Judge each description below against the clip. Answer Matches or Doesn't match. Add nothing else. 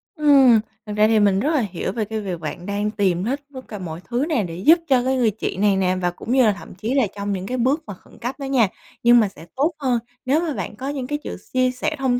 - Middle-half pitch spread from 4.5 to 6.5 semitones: Matches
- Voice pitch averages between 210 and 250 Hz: Matches